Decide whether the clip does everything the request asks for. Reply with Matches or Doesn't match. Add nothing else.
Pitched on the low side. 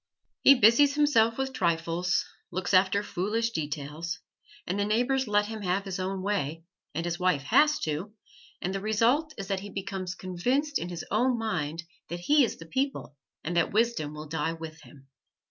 Doesn't match